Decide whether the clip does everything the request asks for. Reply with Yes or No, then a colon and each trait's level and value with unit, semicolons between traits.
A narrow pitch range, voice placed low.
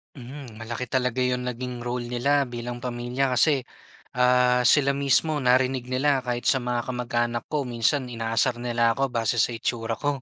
Yes: narrow, 1.7 semitones; low, 125 Hz